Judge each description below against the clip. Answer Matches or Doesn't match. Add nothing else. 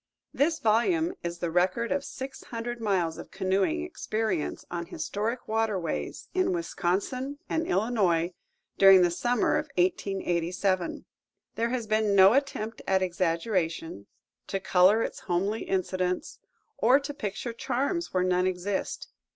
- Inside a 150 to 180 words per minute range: Doesn't match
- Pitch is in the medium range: Doesn't match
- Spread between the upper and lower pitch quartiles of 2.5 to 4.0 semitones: Doesn't match